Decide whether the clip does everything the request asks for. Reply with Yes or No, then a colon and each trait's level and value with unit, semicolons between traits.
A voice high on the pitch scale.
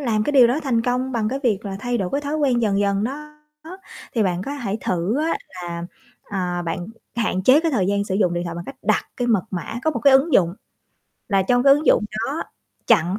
Yes: high, 220 Hz